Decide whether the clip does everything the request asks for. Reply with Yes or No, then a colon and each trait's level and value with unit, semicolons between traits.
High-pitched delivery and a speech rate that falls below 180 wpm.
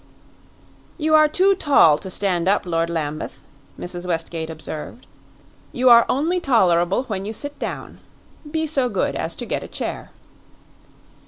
Yes: high, 205 Hz; average, 150 wpm